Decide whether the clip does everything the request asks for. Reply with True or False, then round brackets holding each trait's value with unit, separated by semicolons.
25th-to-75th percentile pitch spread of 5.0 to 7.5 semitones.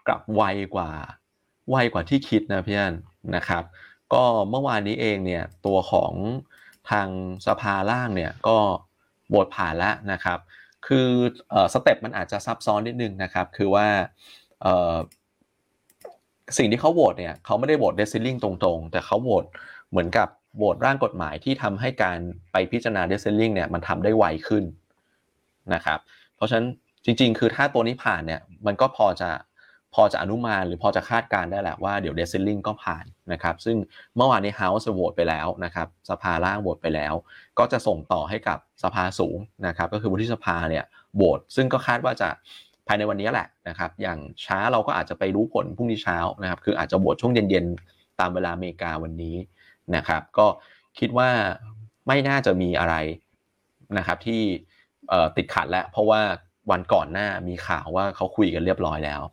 False (3.8 semitones)